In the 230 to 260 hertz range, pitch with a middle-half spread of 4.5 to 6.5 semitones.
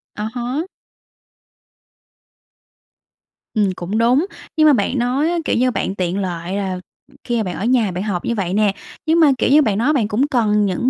No: high, 220 Hz; average, 4.9 semitones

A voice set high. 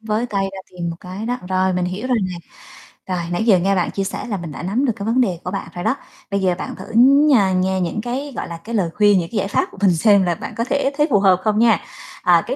Yes: high, 200 Hz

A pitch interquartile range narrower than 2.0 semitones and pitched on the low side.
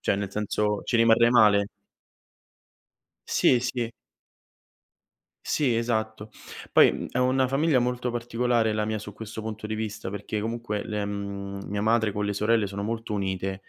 No: narrow, 2.4 semitones; low, 110 Hz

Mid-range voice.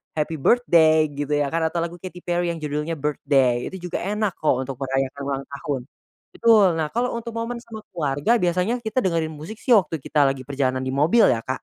Yes: medium, 160 Hz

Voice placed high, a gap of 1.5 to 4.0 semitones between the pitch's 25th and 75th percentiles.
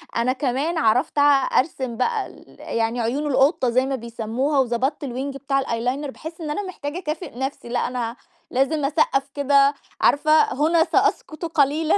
Yes: very high, 275 Hz; average, 3.4 semitones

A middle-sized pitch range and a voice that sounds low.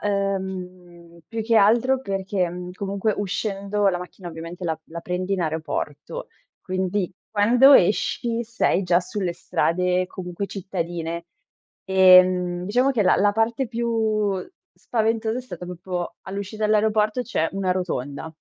No: average, 3.3 semitones; high, 190 Hz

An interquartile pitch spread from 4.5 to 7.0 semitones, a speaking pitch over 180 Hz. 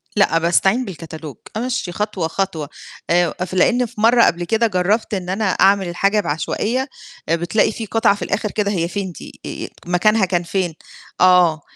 No: average, 3.7 semitones; high, 190 Hz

